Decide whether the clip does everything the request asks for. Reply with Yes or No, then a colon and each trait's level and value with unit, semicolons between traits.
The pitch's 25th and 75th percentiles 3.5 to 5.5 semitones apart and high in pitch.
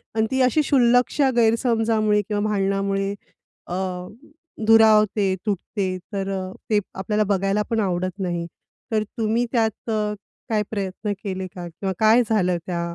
No: average, 2.8 semitones; high, 210 Hz